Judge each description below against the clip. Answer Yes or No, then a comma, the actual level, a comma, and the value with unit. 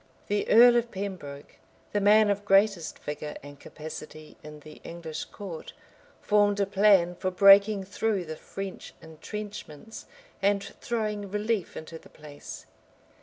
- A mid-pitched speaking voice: No, high, 195 Hz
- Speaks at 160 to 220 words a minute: No, slow, 135 wpm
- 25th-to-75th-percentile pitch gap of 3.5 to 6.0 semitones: Yes, average, 4.5 semitones